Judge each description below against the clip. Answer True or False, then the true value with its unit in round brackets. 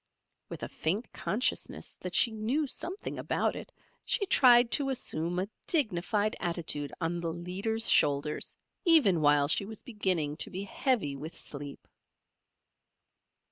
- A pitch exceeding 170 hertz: True (190 Hz)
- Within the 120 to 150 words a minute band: True (140 wpm)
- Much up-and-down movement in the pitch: True (6.7 semitones)